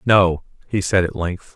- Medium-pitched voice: No, very low, 95 Hz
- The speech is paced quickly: No, average, 195 wpm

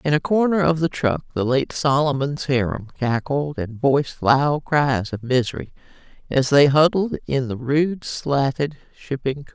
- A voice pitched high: No, medium, 140 Hz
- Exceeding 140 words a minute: Yes, average, 165 wpm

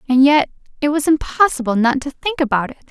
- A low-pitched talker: No, very high, 280 Hz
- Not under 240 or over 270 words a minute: No, fast, 205 wpm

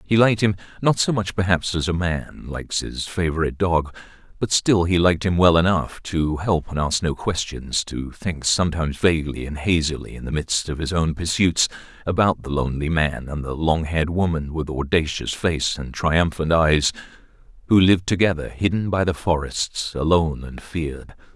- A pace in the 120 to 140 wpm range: No, average, 175 wpm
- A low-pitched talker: Yes, very low, 85 Hz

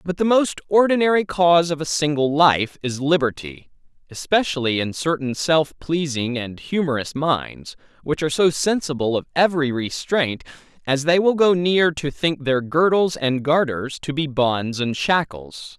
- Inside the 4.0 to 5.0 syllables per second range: Yes, 4.5 syllables/s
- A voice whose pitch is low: No, medium, 150 Hz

